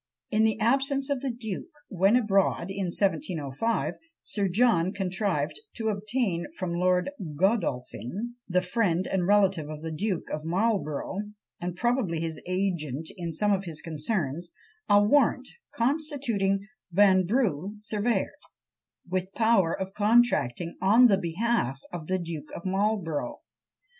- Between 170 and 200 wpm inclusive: No, slow, 135 wpm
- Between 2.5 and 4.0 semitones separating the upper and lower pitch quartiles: No, average, 4.5 semitones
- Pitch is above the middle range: Yes, high, 195 Hz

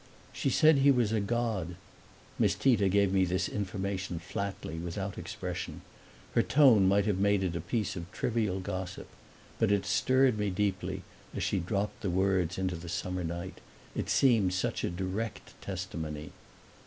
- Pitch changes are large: No, narrow, 2.6 semitones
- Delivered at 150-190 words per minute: Yes, average, 165 wpm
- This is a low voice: Yes, very low, 95 Hz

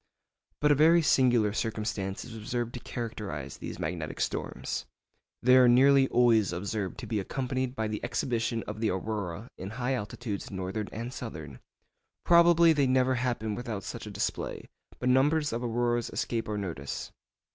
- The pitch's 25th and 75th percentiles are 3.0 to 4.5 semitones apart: Yes, average, 3.5 semitones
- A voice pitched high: No, low, 115 Hz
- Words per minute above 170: No, average, 160 wpm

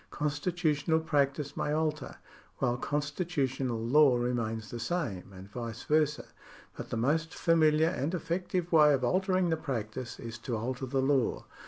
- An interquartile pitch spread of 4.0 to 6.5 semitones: Yes, average, 4.8 semitones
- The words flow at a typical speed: Yes, average, 150 wpm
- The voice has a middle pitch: Yes, medium, 145 Hz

